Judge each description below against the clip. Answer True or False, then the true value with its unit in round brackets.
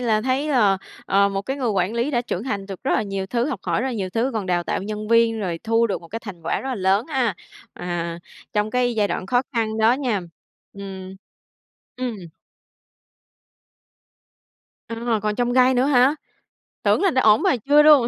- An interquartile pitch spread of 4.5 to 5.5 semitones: False (4.1 semitones)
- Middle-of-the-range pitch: False (225 Hz)